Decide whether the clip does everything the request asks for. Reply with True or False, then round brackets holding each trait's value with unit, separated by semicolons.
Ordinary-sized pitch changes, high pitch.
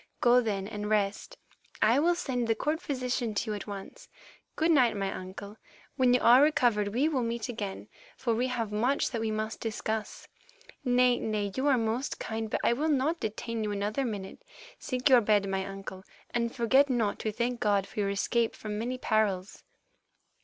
True (3.3 semitones; 225 Hz)